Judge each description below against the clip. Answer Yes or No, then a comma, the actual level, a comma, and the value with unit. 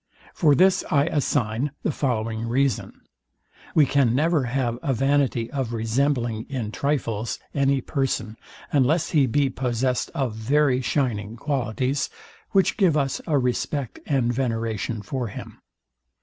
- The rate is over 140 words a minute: No, slow, 135 wpm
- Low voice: Yes, low, 130 Hz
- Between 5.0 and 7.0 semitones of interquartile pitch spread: No, average, 3.5 semitones